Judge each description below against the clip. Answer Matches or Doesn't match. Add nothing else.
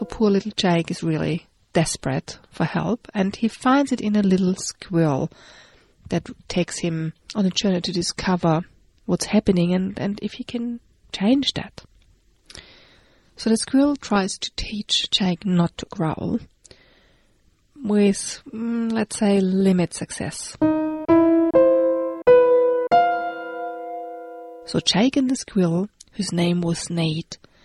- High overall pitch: Matches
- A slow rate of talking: Matches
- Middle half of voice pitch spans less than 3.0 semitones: Doesn't match